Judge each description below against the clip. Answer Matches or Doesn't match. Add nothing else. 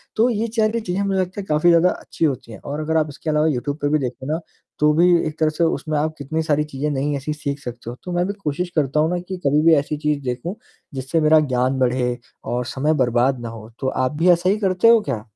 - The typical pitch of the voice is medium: Matches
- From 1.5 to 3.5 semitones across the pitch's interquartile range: Doesn't match